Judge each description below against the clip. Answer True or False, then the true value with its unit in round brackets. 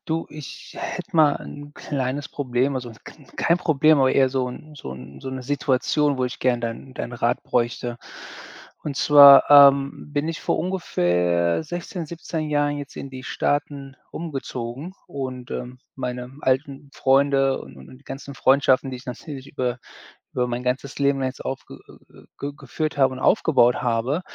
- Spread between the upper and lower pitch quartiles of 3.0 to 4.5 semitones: False (2.5 semitones)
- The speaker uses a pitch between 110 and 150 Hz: True (135 Hz)